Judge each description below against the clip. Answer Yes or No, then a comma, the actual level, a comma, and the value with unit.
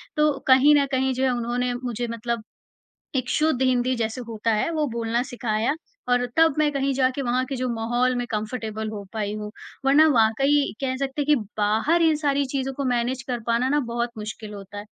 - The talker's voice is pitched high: Yes, very high, 250 Hz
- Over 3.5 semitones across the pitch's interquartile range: No, average, 3.2 semitones